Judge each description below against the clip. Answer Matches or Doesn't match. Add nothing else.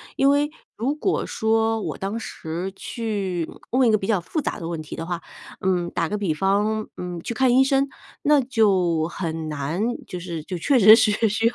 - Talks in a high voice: Matches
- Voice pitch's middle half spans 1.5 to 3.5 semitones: Doesn't match